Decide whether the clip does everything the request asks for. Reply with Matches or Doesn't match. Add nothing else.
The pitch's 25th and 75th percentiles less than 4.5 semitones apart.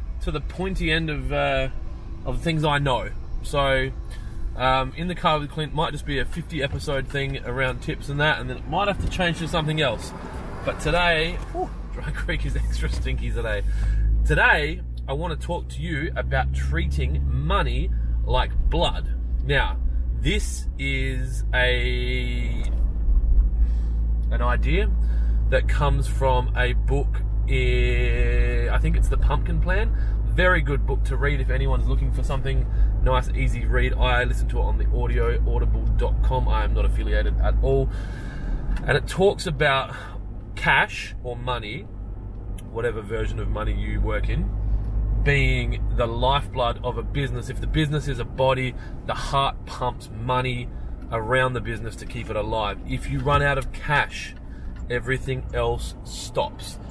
Doesn't match